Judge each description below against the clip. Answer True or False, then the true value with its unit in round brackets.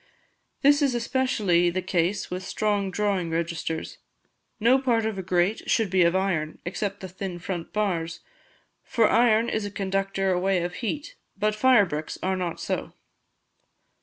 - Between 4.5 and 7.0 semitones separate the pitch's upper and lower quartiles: False (3.6 semitones)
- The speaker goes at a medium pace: True (160 wpm)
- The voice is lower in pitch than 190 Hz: False (195 Hz)